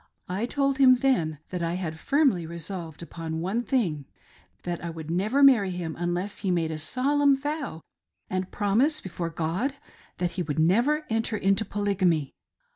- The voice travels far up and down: Yes, wide, 7.1 semitones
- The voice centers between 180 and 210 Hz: Yes, medium, 185 Hz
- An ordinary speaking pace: Yes, average, 165 wpm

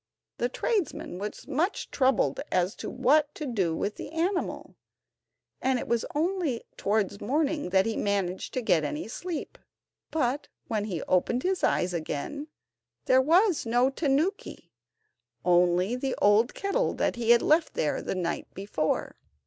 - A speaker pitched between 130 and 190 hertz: No, high, 245 Hz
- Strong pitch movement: Yes, wide, 7.5 semitones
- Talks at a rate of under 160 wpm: Yes, average, 150 wpm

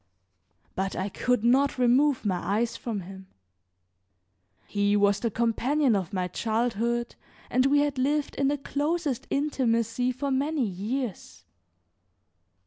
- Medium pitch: No, high, 240 Hz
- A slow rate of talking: Yes, slow, 130 wpm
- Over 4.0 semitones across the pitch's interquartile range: Yes, average, 5.2 semitones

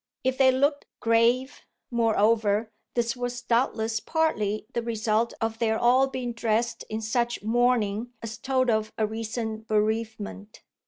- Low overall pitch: No, high, 230 Hz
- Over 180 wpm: No, average, 140 wpm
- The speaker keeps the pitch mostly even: Yes, narrow, 2.0 semitones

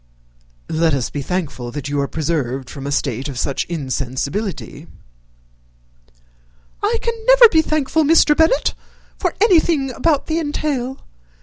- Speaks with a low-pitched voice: No, medium, 185 Hz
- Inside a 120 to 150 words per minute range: Yes, slow, 135 wpm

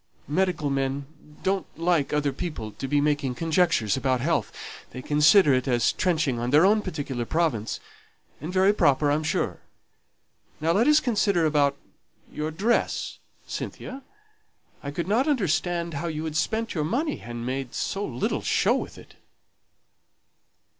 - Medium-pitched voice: Yes, medium, 155 Hz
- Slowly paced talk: No, average, 150 wpm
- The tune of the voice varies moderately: Yes, average, 4.7 semitones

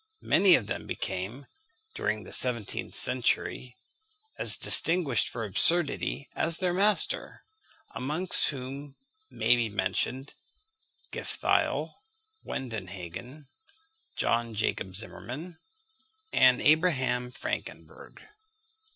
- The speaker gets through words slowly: Yes, slow, 90 wpm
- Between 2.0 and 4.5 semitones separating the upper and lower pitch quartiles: No, wide, 5.4 semitones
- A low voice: Yes, low, 130 Hz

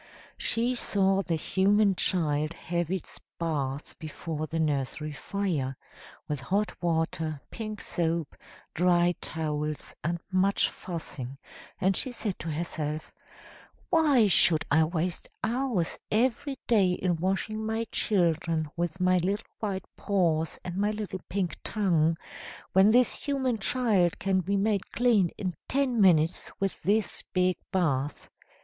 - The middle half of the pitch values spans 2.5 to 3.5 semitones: No, average, 4.3 semitones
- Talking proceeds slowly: Yes, slow, 130 wpm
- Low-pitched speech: No, medium, 180 Hz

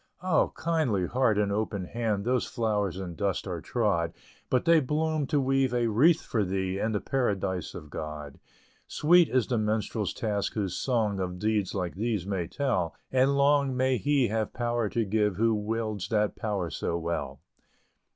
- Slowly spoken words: No, average, 175 wpm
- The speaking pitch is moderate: No, low, 110 Hz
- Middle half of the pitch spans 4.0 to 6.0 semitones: Yes, average, 4.9 semitones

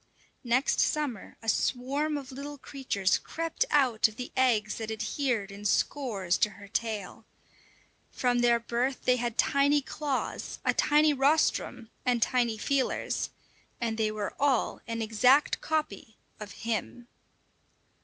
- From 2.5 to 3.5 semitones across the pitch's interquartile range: No, average, 4.1 semitones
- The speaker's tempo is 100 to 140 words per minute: Yes, slow, 135 wpm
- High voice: Yes, high, 245 Hz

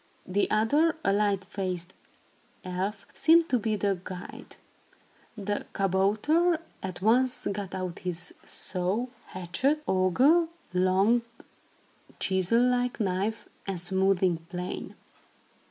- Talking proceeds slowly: Yes, slow, 105 wpm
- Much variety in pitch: No, average, 4.2 semitones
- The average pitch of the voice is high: Yes, high, 195 Hz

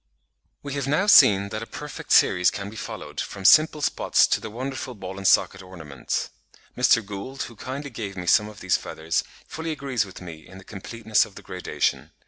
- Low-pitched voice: Yes, low, 105 Hz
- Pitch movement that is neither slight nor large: No, wide, 5.8 semitones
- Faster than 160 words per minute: Yes, average, 200 wpm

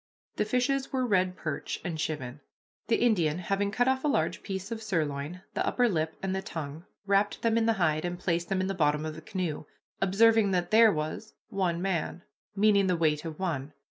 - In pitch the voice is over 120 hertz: Yes, medium, 185 Hz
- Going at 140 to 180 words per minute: No, fast, 205 wpm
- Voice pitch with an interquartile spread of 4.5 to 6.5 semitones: Yes, average, 5.1 semitones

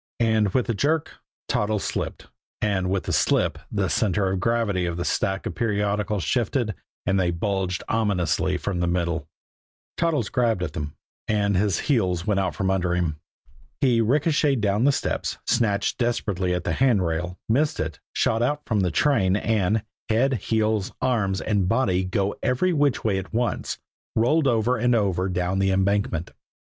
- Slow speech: No, average, 170 wpm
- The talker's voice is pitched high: No, low, 100 Hz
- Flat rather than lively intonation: No, average, 4.2 semitones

